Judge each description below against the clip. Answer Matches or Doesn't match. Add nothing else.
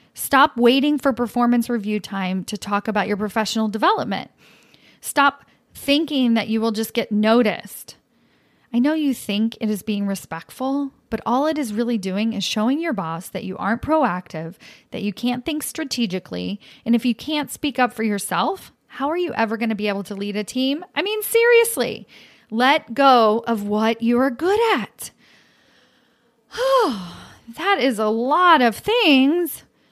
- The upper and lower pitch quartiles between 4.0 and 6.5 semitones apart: Matches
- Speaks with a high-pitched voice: Matches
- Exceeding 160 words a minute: Matches